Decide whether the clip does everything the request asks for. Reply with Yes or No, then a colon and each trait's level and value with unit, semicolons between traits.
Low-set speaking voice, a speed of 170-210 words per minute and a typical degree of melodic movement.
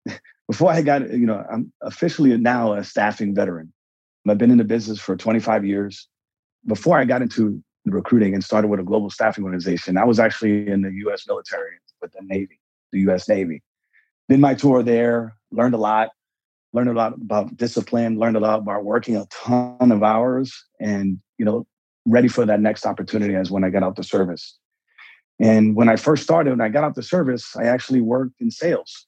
Yes: low, 115 Hz; average, 200 wpm; average, 3.3 semitones